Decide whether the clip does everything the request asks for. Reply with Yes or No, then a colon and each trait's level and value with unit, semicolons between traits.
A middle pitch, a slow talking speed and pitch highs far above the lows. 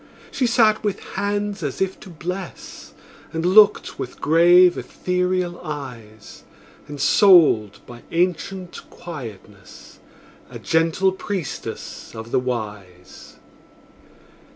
Yes: medium, 170 Hz; slow, 100 wpm; wide, 7.5 semitones